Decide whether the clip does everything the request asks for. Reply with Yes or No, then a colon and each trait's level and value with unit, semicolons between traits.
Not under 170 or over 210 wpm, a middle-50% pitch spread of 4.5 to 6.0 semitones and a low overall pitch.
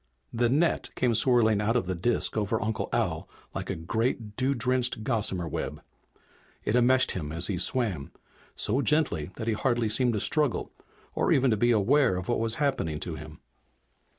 No: average, 180 wpm; average, 3.7 semitones; low, 115 Hz